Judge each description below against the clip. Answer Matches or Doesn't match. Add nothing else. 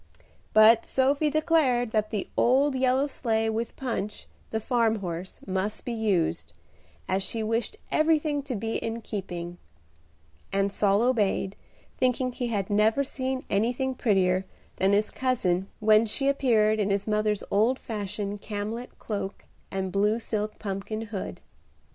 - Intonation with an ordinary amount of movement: Matches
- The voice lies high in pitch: Matches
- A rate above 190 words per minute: Doesn't match